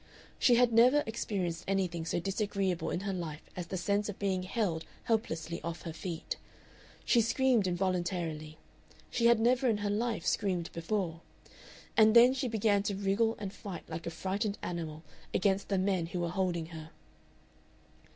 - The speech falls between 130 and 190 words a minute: Yes, average, 165 wpm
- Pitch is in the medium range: No, high, 195 Hz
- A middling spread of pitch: Yes, average, 4.1 semitones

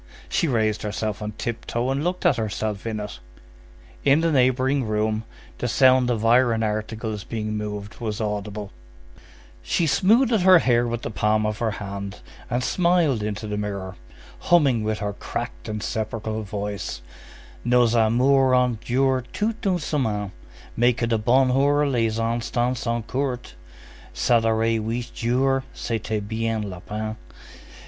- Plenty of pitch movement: No, average, 3.2 semitones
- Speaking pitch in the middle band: No, low, 115 Hz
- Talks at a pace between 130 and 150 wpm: Yes, average, 145 wpm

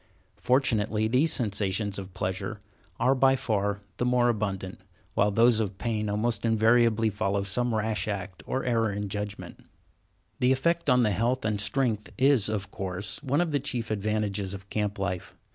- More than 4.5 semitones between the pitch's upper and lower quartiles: No, average, 3.3 semitones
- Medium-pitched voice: No, low, 110 Hz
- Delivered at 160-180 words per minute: Yes, average, 165 wpm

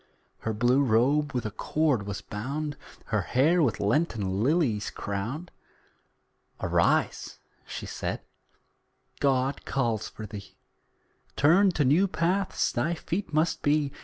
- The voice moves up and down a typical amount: No, wide, 6.0 semitones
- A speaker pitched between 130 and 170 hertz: Yes, medium, 140 Hz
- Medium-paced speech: No, slow, 125 wpm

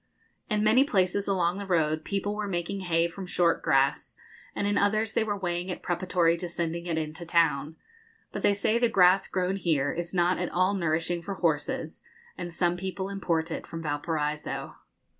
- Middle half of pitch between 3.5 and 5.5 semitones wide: No, average, 2.9 semitones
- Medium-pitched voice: Yes, medium, 175 Hz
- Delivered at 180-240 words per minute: Yes, average, 185 wpm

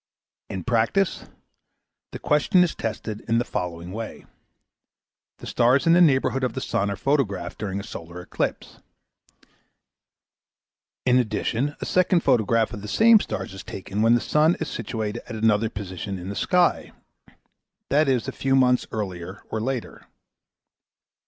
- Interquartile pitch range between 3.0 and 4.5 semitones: No, average, 5.0 semitones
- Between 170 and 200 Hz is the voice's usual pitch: No, low, 115 Hz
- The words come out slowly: No, average, 150 wpm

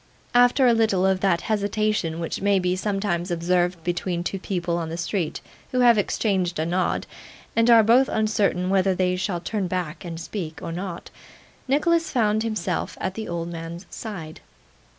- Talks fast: No, average, 170 wpm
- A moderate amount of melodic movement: Yes, average, 3.8 semitones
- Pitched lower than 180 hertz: No, medium, 185 Hz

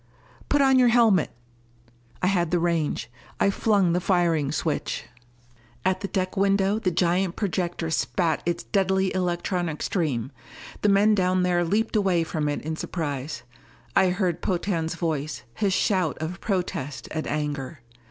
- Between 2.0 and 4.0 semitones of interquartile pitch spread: Yes, average, 3.3 semitones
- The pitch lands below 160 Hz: No, medium, 180 Hz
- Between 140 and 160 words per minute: Yes, average, 150 wpm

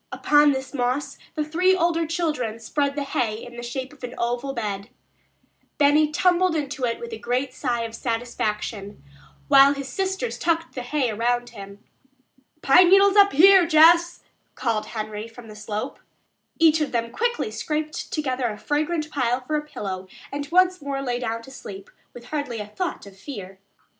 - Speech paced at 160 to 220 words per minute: Yes, average, 175 wpm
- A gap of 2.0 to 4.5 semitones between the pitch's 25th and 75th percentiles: No, average, 5.0 semitones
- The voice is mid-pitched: No, very high, 265 Hz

